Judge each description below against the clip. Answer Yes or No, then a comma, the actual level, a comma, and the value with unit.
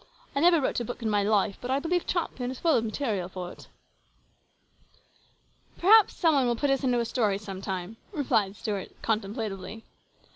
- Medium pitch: No, high, 225 Hz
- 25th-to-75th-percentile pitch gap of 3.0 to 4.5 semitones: No, average, 5.3 semitones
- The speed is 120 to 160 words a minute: No, average, 190 wpm